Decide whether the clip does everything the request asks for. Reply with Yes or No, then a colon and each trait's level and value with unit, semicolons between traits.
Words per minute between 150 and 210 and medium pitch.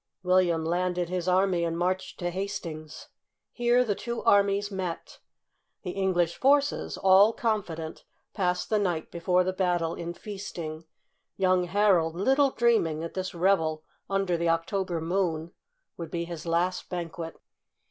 No: average, 140 wpm; medium, 180 Hz